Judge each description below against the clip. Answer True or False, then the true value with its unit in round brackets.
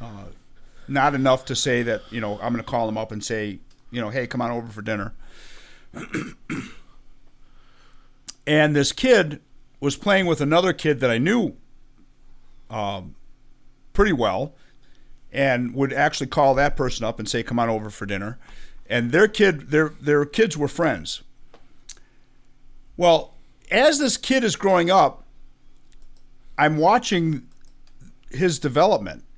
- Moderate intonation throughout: True (3.9 semitones)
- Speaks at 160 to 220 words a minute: False (145 wpm)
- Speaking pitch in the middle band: False (130 Hz)